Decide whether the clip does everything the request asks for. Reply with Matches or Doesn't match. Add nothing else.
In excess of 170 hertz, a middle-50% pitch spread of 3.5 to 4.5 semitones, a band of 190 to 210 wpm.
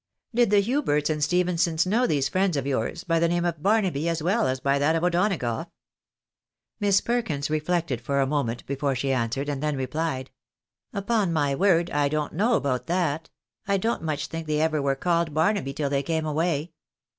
Doesn't match